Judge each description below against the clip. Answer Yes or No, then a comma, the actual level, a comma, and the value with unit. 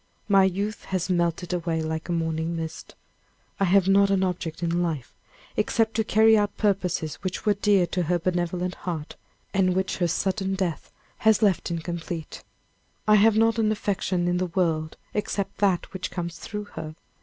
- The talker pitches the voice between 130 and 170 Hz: No, medium, 185 Hz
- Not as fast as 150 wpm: No, average, 175 wpm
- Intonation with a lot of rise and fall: No, average, 2.9 semitones